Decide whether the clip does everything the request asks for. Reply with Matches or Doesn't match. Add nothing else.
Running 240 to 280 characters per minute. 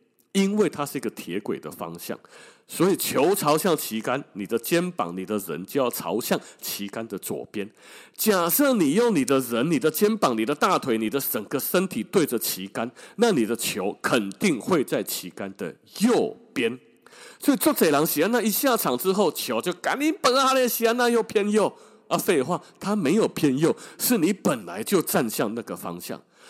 Matches